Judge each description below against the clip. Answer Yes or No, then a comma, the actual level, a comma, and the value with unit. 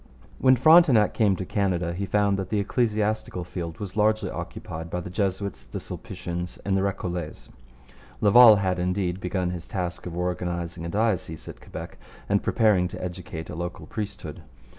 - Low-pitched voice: Yes, very low, 95 Hz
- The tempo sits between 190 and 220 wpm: No, average, 165 wpm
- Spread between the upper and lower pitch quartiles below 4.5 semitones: Yes, average, 2.9 semitones